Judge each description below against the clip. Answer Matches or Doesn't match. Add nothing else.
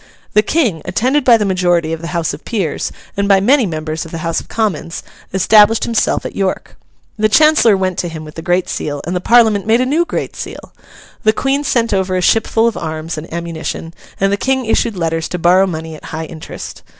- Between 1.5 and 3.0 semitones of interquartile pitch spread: Doesn't match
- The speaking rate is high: Matches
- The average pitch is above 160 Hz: Matches